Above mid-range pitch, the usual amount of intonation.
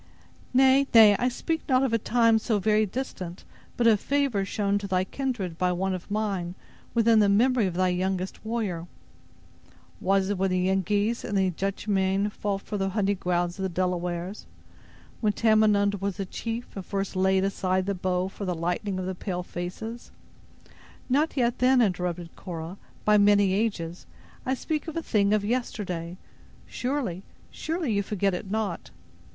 Yes: high, 200 Hz; average, 3.4 semitones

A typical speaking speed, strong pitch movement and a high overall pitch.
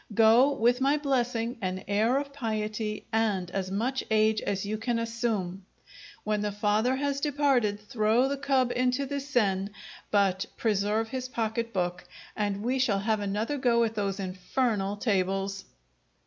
No: average, 155 wpm; average, 3.8 semitones; high, 220 Hz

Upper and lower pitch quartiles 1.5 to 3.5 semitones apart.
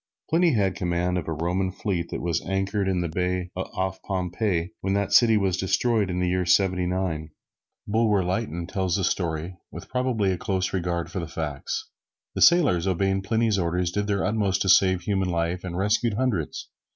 Yes: narrow, 2.5 semitones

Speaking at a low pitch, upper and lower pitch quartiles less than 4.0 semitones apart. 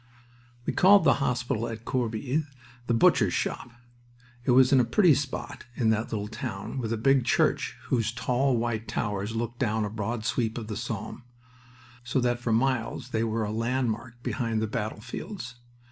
Yes: low, 115 Hz; narrow, 2.4 semitones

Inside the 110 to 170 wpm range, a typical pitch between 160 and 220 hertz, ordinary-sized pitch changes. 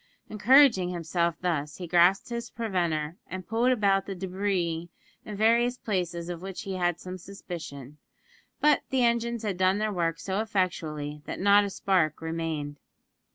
Yes: average, 155 wpm; medium, 185 Hz; average, 3.8 semitones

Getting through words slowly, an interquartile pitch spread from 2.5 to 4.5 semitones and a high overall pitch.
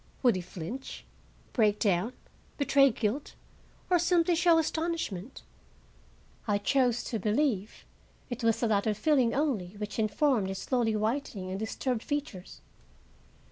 No: slow, 130 wpm; wide, 5.4 semitones; high, 230 Hz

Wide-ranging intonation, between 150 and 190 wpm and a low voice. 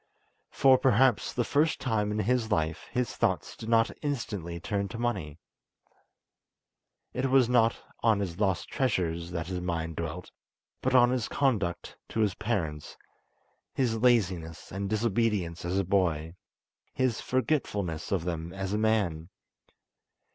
No: wide, 5.7 semitones; average, 140 wpm; low, 105 Hz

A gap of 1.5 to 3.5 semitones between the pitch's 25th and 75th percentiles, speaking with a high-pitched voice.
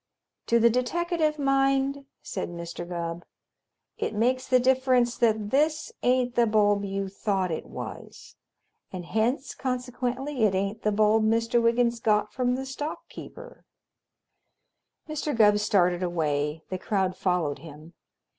No: average, 5.3 semitones; high, 225 Hz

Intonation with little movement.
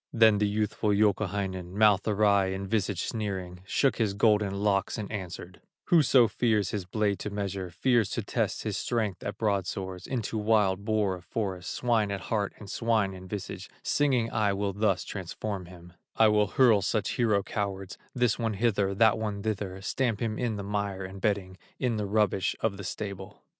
Yes: narrow, 2.1 semitones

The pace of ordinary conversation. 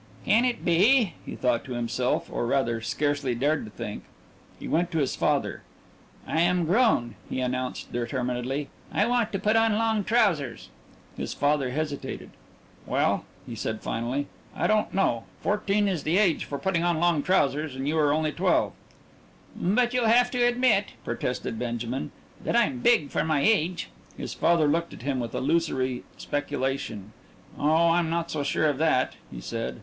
Yes: average, 175 wpm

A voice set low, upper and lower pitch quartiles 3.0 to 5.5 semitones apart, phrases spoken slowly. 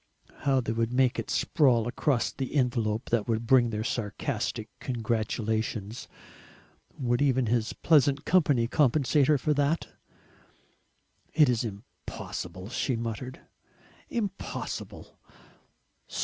Yes: low, 120 Hz; average, 3.6 semitones; slow, 110 wpm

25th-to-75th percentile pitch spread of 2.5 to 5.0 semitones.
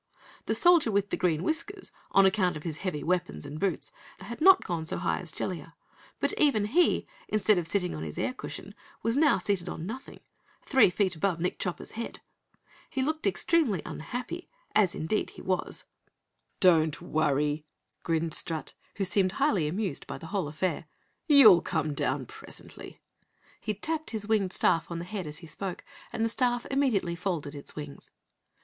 No: wide, 5.5 semitones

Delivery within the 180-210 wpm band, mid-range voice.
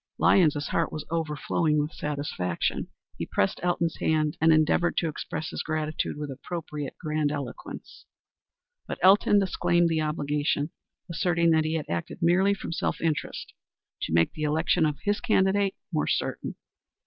No: average, 150 wpm; medium, 155 Hz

